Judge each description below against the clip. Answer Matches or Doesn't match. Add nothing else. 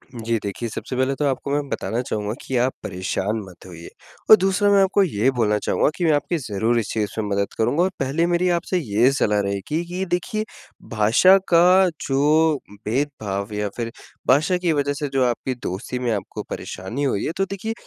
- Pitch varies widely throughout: Matches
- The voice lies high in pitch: Doesn't match